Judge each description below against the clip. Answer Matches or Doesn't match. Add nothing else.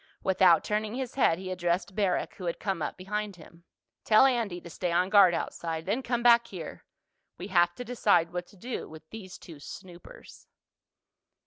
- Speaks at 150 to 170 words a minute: Doesn't match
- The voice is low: Doesn't match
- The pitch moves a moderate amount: Matches